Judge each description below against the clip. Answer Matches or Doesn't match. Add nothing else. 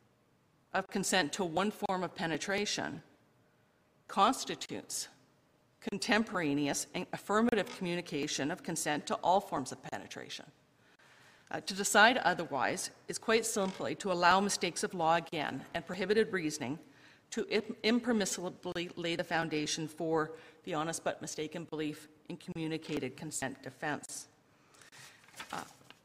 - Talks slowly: Matches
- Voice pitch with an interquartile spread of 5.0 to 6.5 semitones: Doesn't match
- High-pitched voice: Doesn't match